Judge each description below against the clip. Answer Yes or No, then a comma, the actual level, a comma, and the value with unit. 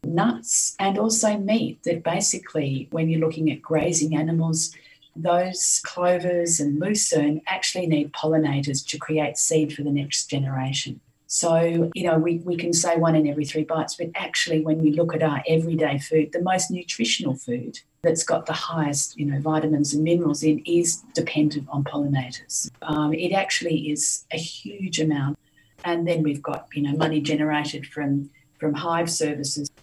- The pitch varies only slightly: Yes, narrow, 2.3 semitones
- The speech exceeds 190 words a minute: No, average, 170 wpm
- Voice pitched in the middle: Yes, medium, 155 Hz